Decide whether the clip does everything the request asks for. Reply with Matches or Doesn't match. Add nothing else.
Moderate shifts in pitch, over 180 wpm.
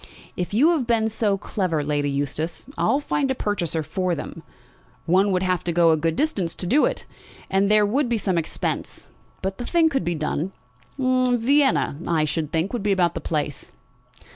Doesn't match